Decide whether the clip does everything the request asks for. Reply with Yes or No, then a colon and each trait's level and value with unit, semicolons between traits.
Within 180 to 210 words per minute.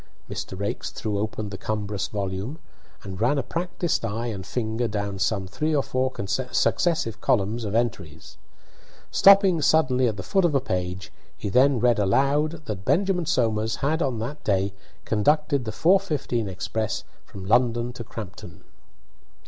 No: average, 155 wpm